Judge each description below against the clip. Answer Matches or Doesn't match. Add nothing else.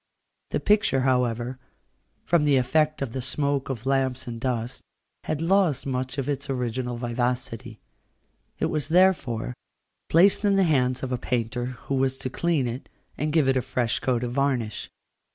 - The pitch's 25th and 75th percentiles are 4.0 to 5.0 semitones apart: Doesn't match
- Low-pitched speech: Matches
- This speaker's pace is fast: Doesn't match